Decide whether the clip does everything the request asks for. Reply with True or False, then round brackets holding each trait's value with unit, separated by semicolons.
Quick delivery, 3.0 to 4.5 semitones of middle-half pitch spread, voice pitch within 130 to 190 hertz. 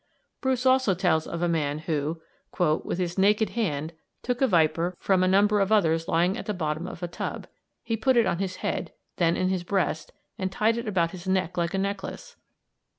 True (210 wpm; 3.7 semitones; 185 Hz)